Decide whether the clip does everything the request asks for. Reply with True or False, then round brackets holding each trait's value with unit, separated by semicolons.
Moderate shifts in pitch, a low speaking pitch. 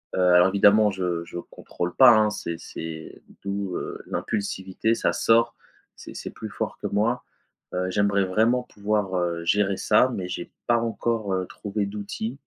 True (3.0 semitones; 100 Hz)